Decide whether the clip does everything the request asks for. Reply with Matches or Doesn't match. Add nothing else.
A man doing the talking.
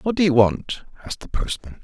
Matches